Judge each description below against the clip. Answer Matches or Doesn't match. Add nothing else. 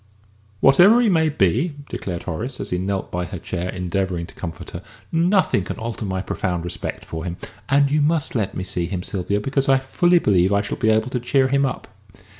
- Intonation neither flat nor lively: Doesn't match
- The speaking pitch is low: Matches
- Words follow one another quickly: Matches